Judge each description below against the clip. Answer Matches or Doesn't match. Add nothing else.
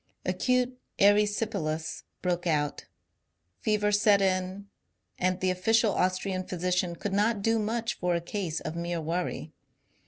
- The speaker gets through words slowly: Matches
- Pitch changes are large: Doesn't match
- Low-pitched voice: Doesn't match